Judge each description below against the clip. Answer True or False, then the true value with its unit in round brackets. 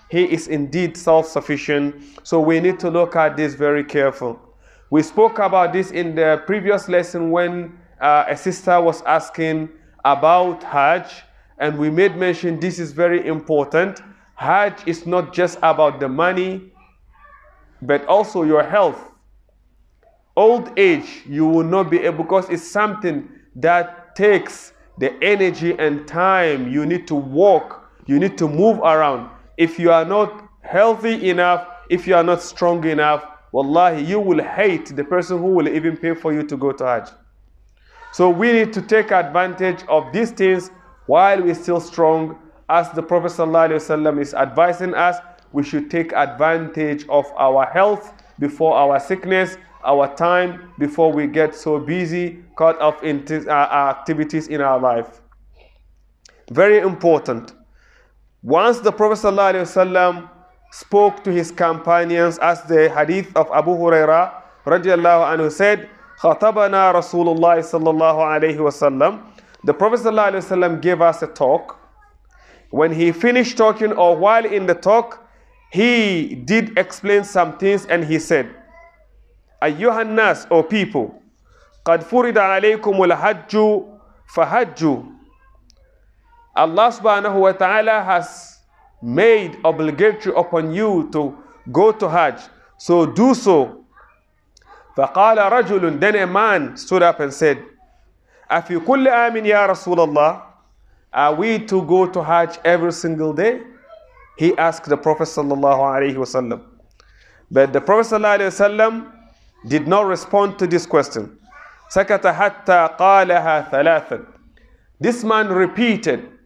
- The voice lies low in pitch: False (175 Hz)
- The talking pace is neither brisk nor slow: False (130 wpm)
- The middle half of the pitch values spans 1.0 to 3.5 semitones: False (4.3 semitones)